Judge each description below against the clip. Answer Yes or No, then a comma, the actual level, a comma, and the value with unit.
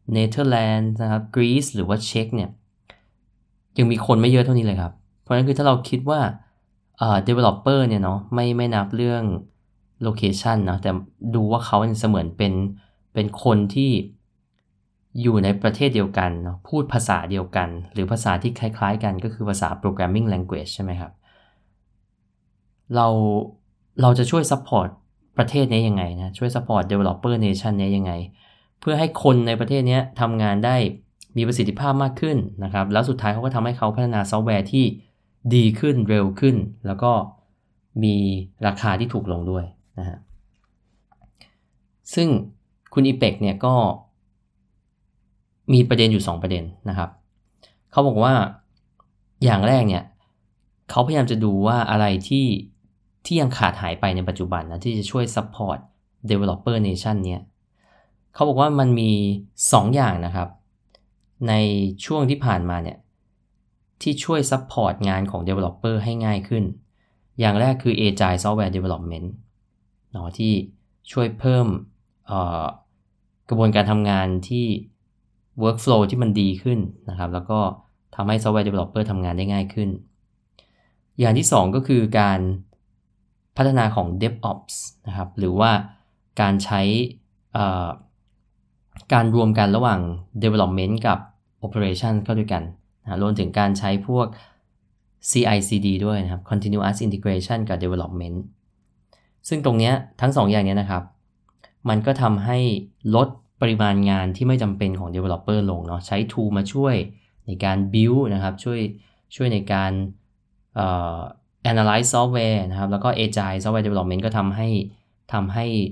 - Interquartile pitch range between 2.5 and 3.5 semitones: Yes, average, 2.9 semitones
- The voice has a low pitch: Yes, low, 105 Hz